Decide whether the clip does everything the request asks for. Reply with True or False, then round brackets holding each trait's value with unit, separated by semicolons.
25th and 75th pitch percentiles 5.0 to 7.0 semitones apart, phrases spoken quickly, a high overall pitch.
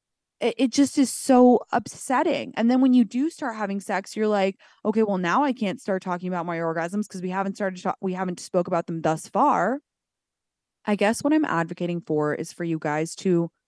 True (5.4 semitones; 215 wpm; 195 Hz)